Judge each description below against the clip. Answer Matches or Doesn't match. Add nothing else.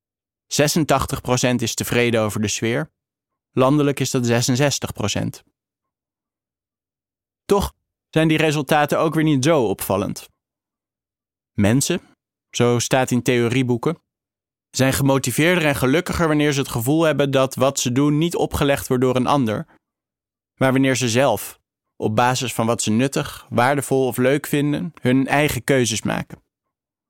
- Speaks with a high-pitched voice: Doesn't match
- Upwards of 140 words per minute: Doesn't match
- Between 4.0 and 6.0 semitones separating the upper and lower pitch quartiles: Doesn't match